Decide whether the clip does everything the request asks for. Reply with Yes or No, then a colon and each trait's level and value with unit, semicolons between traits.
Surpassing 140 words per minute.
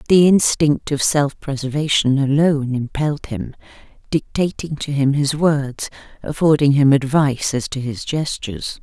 No: slow, 135 wpm